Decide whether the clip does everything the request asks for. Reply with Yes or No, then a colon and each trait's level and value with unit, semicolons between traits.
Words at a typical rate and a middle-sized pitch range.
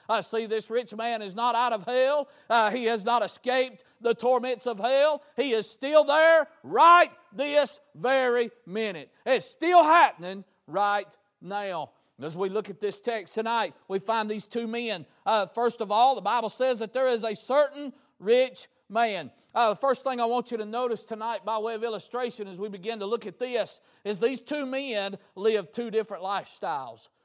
Yes: average, 195 wpm; average, 3.3 semitones